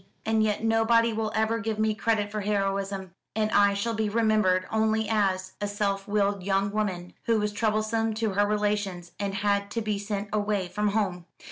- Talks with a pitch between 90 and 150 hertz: No, high, 210 Hz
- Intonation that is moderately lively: No, narrow, 1.6 semitones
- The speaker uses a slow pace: No, average, 190 wpm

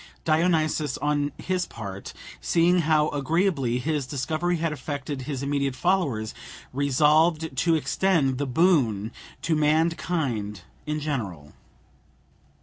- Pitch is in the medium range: Yes, medium, 150 Hz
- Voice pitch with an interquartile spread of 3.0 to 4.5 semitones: Yes, average, 3.9 semitones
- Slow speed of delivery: Yes, slow, 110 wpm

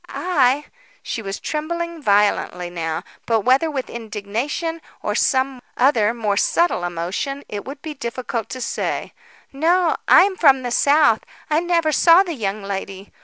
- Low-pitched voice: No, very high, 260 Hz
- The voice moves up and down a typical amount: No, wide, 7.1 semitones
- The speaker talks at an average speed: Yes, average, 150 wpm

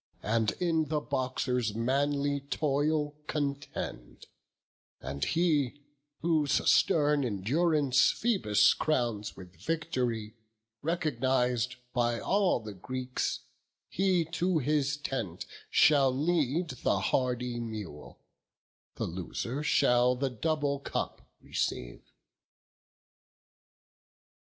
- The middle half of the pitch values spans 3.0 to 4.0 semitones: No, average, 4.4 semitones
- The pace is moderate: No, slow, 90 wpm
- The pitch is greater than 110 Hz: Yes, low, 135 Hz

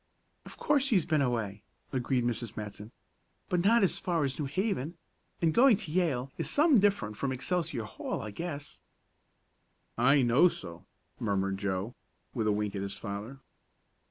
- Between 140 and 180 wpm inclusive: Yes, average, 160 wpm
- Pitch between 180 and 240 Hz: No, low, 135 Hz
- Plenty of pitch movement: Yes, wide, 8.8 semitones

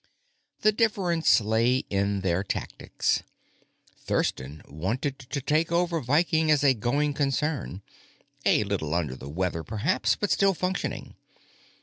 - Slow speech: Yes, slow, 125 wpm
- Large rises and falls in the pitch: Yes, wide, 8.6 semitones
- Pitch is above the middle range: No, low, 130 Hz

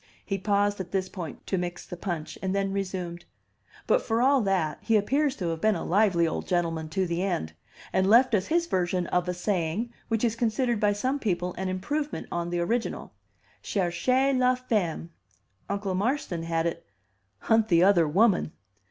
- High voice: Yes, high, 195 Hz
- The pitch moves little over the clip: No, average, 4.5 semitones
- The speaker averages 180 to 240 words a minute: Yes, average, 185 wpm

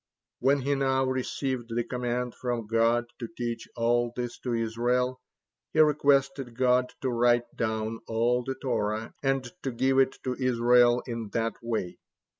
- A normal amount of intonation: No, narrow, 1.9 semitones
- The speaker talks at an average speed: Yes, average, 155 wpm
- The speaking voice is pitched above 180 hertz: No, low, 120 Hz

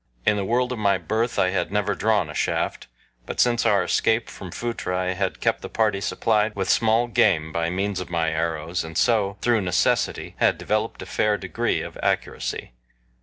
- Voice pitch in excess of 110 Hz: No, low, 100 Hz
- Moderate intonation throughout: Yes, average, 3.7 semitones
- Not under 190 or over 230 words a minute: Yes, average, 195 wpm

